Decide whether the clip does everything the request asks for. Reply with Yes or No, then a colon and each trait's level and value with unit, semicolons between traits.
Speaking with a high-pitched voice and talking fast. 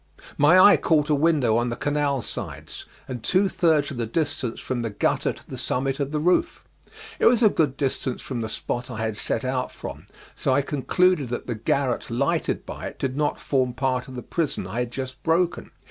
No: low, 135 Hz; fast, 215 wpm